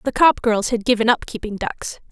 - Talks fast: Yes, fast, 225 wpm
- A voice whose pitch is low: No, high, 230 Hz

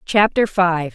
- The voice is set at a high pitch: No, medium, 180 Hz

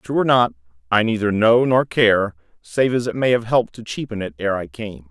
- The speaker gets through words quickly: Yes, fast, 235 wpm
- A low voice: Yes, low, 110 Hz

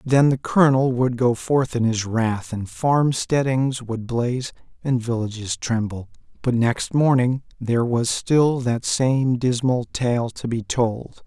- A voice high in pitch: No, low, 125 Hz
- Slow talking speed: No, average, 155 wpm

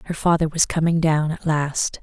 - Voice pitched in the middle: Yes, medium, 160 Hz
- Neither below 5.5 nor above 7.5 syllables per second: No, 4.9 syllables/s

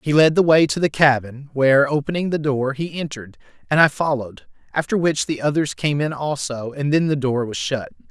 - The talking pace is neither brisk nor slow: No, fast, 215 wpm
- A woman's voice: No, male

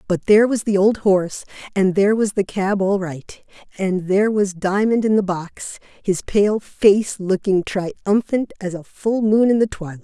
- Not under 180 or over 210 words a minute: Yes, average, 190 wpm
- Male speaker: No, female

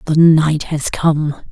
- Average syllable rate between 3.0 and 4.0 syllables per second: Yes, 3.1 syllables/s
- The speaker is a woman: Yes, female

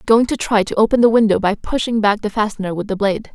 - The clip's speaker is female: Yes, female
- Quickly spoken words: Yes, fast, 285 wpm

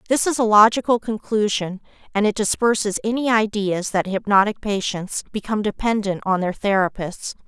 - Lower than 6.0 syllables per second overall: Yes, 5.2 syllables/s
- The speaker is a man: No, female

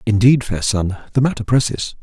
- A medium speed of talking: Yes, average, 180 wpm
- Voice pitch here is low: Yes, low, 115 Hz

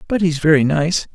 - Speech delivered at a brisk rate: Yes, fast, 210 wpm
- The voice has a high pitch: No, medium, 160 Hz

